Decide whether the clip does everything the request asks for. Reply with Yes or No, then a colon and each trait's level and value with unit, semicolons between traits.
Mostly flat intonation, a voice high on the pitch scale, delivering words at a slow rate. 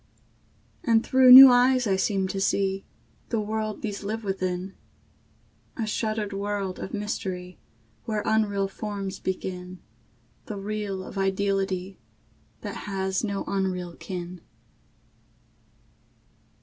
Yes: narrow, 2.0 semitones; high, 200 Hz; slow, 110 wpm